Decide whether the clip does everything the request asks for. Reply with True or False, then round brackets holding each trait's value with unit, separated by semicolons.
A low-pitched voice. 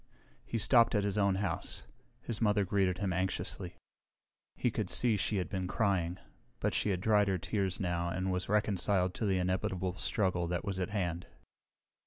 True (95 Hz)